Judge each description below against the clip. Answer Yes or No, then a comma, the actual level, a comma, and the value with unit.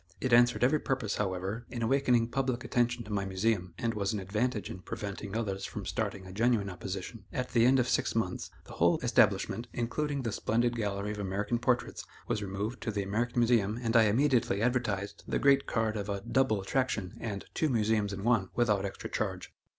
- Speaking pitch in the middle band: No, low, 110 Hz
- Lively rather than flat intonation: No, average, 3.4 semitones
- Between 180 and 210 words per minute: Yes, average, 195 wpm